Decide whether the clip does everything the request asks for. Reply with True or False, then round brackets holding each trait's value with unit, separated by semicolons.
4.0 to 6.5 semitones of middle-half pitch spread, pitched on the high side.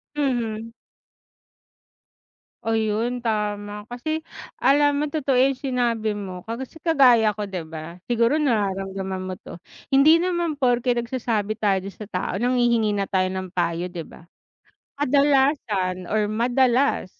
True (4.9 semitones; 230 Hz)